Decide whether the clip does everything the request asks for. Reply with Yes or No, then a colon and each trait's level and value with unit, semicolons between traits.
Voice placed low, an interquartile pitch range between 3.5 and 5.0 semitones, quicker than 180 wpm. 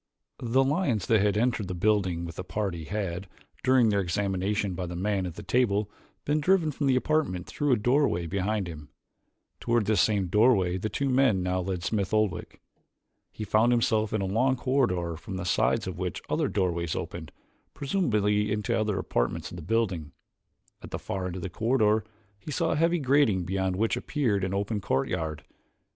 Yes: low, 105 Hz; average, 4.5 semitones; average, 190 wpm